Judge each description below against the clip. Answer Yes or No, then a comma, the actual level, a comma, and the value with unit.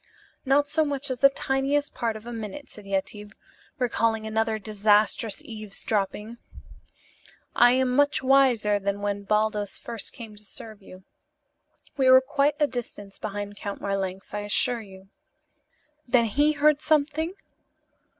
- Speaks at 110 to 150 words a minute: Yes, average, 140 wpm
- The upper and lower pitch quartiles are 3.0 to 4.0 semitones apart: No, average, 4.6 semitones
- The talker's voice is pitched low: No, high, 225 Hz